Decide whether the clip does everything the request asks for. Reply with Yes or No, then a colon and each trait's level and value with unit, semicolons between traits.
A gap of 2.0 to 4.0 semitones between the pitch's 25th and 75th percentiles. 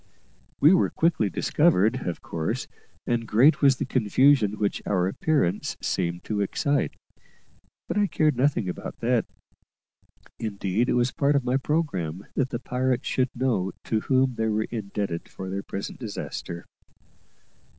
No: average, 5.2 semitones